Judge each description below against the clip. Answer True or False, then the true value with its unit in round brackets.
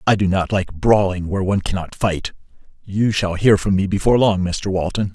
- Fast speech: True (210 wpm)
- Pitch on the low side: True (95 Hz)